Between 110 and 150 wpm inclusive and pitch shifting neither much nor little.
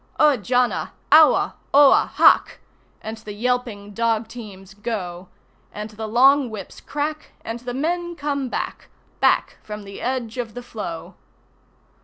Yes: average, 140 wpm; average, 4.2 semitones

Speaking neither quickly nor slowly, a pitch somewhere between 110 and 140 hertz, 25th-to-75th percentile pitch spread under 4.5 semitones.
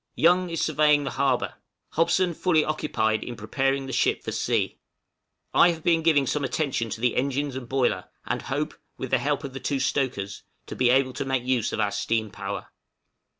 Yes: average, 195 wpm; low, 135 Hz; average, 3.7 semitones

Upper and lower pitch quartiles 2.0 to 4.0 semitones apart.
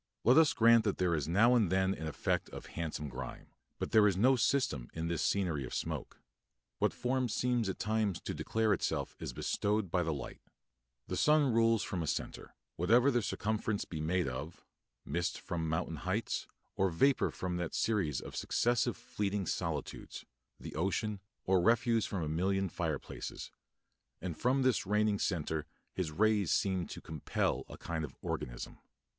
No: wide, 5.4 semitones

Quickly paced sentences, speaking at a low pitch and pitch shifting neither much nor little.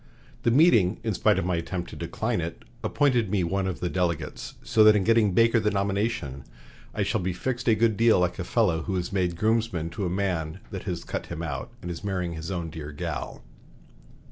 Yes: fast, 220 wpm; very low, 95 Hz; average, 4.1 semitones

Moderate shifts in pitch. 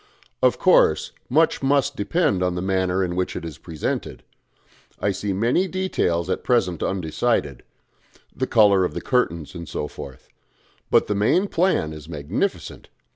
No: wide, 6.8 semitones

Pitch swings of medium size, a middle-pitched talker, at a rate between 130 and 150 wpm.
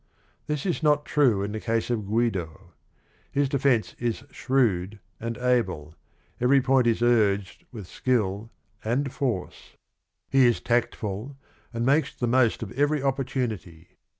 No: average, 4.3 semitones; low, 120 Hz; average, 140 wpm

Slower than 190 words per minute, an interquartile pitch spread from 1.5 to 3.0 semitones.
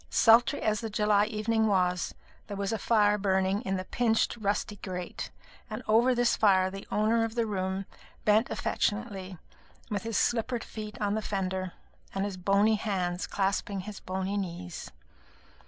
Yes: average, 160 wpm; narrow, 2.5 semitones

